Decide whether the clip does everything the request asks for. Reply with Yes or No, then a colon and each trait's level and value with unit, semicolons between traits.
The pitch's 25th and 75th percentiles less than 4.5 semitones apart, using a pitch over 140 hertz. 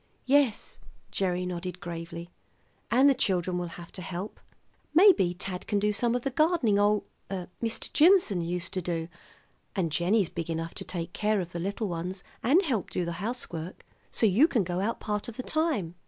No: average, 5.0 semitones; high, 190 Hz